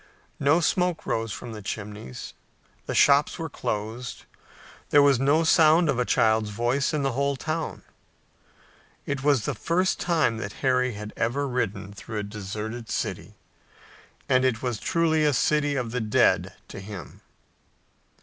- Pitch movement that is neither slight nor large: Yes, average, 5.0 semitones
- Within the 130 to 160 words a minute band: Yes, average, 155 wpm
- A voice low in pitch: Yes, low, 125 Hz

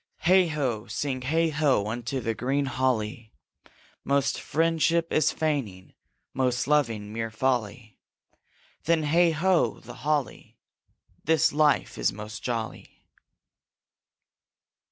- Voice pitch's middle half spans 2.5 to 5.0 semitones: No, wide, 5.4 semitones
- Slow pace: Yes, slow, 110 wpm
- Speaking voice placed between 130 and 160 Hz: Yes, low, 135 Hz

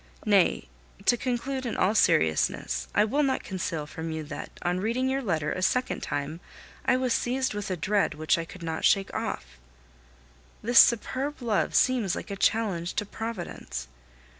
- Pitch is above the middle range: Yes, high, 200 Hz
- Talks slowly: No, average, 170 wpm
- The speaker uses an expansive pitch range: Yes, wide, 7.1 semitones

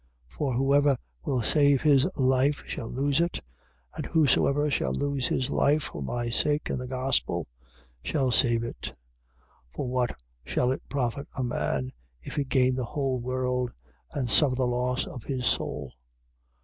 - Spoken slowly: No, average, 165 wpm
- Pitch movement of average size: No, narrow, 2.3 semitones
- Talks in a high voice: No, low, 130 Hz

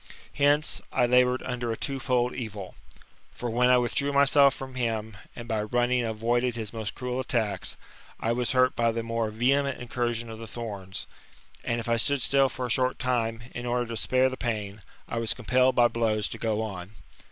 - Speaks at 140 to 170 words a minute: No, average, 200 wpm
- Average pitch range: No, narrow, 2.1 semitones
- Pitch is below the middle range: Yes, low, 120 Hz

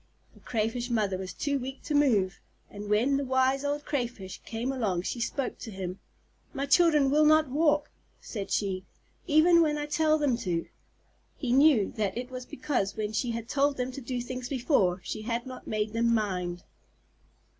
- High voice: Yes, very high, 250 Hz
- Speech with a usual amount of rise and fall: Yes, average, 5.0 semitones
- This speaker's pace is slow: No, average, 185 wpm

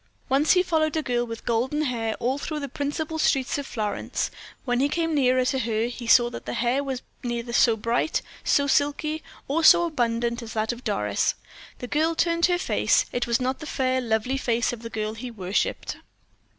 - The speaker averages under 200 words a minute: No, fast, 205 wpm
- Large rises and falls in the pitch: No, average, 3.9 semitones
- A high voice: Yes, very high, 250 Hz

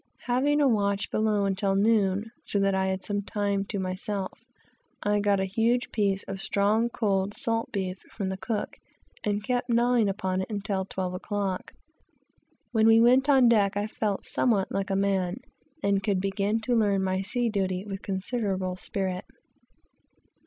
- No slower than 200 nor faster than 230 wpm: No, average, 170 wpm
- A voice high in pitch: Yes, high, 200 Hz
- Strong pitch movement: No, narrow, 2.6 semitones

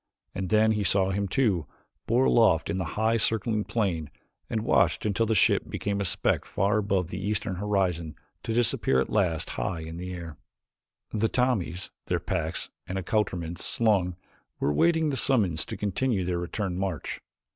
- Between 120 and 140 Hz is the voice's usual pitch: No, low, 100 Hz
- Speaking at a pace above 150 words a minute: Yes, average, 170 wpm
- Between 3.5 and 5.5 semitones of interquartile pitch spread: Yes, average, 3.8 semitones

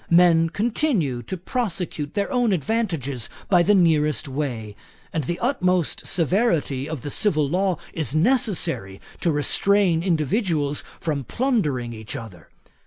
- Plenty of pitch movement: Yes, wide, 5.7 semitones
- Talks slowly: Yes, slow, 130 wpm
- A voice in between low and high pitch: Yes, medium, 165 Hz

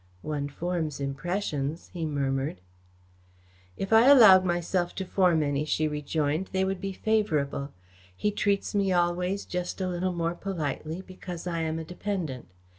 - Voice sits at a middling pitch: Yes, medium, 175 Hz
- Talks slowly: No, average, 150 wpm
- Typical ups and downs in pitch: Yes, average, 3.9 semitones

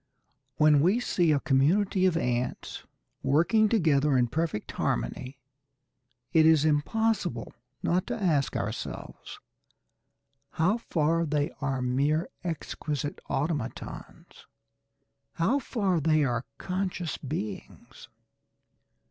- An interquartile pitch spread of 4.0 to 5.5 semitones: Yes, average, 4.6 semitones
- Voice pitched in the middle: Yes, medium, 155 Hz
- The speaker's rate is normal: No, slow, 100 wpm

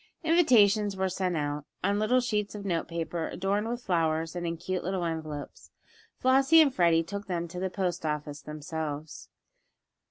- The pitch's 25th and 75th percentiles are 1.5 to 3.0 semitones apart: No, average, 4.2 semitones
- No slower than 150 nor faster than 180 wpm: Yes, average, 165 wpm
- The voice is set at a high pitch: No, medium, 180 Hz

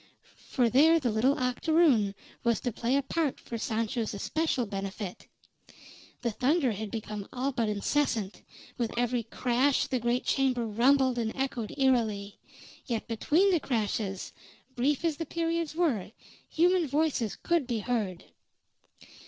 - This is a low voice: No, high, 245 Hz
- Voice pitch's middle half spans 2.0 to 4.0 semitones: No, average, 4.5 semitones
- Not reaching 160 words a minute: Yes, average, 140 wpm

